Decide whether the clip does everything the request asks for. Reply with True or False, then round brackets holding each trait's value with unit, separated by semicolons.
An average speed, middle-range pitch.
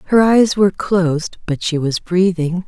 True (180 wpm; 180 Hz)